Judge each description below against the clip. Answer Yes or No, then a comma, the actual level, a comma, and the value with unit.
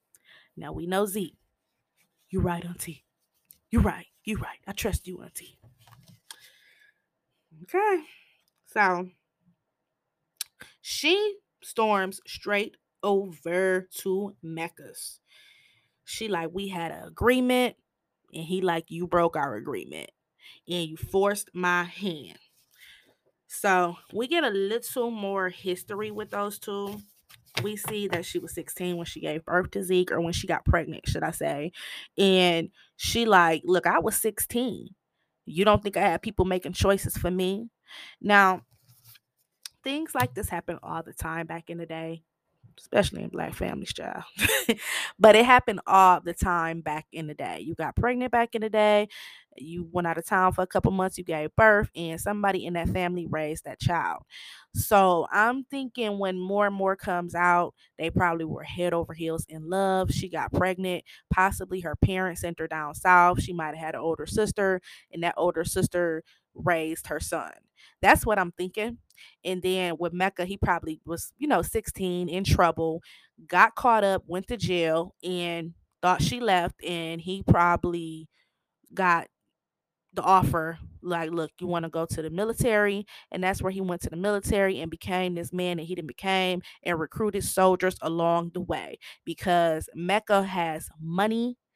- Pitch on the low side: No, medium, 180 Hz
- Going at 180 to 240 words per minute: No, average, 165 wpm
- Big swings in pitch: No, average, 3.2 semitones